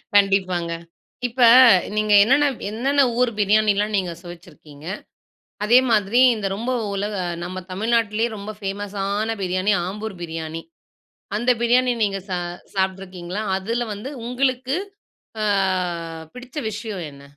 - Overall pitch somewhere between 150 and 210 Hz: Yes, high, 205 Hz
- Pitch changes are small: No, average, 3.6 semitones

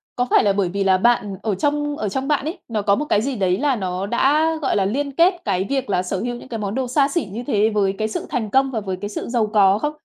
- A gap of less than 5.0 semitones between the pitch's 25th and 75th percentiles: No, wide, 5.4 semitones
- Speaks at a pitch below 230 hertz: Yes, high, 220 Hz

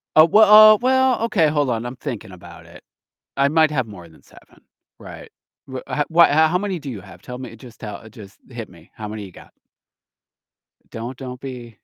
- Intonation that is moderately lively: No, wide, 6.2 semitones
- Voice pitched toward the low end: Yes, low, 130 Hz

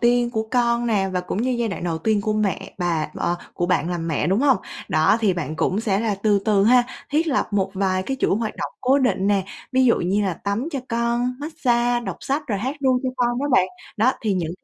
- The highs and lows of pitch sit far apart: No, average, 4.5 semitones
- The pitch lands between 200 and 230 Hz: Yes, high, 220 Hz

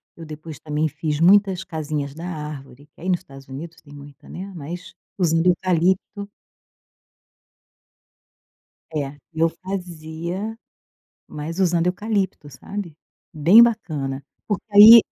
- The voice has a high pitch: No, medium, 165 Hz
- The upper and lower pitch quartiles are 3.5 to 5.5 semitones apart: Yes, average, 3.9 semitones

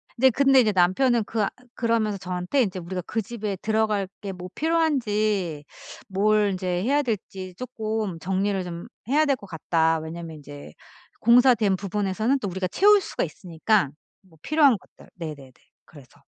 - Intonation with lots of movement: No, average, 4.5 semitones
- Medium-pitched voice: No, high, 200 Hz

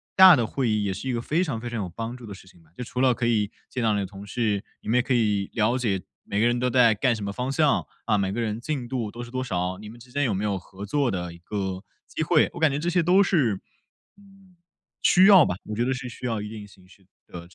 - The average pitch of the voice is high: No, low, 115 Hz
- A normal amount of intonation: Yes, average, 4.3 semitones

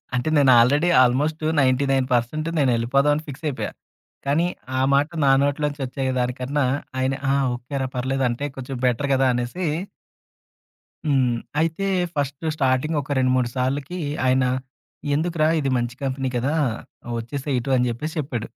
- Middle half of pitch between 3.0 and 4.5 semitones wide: No, narrow, 2.4 semitones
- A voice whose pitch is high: No, low, 135 Hz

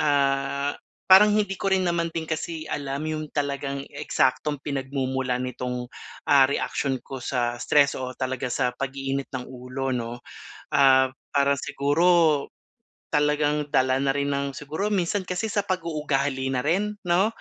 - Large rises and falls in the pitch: No, average, 2.9 semitones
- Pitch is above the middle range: No, medium, 140 Hz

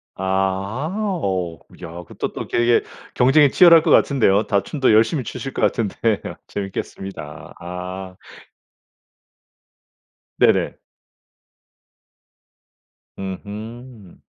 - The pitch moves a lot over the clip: No, average, 4.5 semitones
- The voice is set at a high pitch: No, low, 100 Hz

